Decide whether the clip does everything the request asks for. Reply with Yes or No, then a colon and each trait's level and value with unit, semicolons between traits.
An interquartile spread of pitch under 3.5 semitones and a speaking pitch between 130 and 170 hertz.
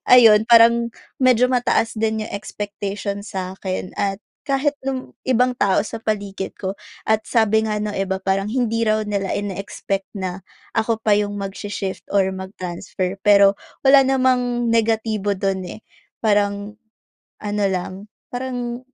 No: average, 2.9 semitones; high, 210 Hz